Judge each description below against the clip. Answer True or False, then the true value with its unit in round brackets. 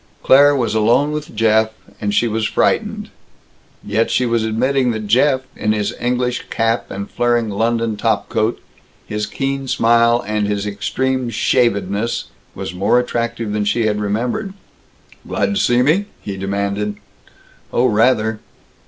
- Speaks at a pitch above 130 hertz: False (115 Hz)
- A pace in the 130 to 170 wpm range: True (145 wpm)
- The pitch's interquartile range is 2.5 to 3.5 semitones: True (2.9 semitones)